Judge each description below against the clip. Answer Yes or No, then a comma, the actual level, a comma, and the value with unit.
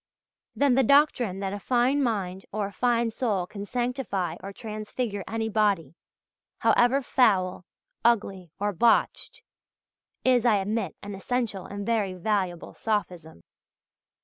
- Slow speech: Yes, slow, 130 wpm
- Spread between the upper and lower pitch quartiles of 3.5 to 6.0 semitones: Yes, average, 3.9 semitones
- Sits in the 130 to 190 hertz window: No, high, 210 Hz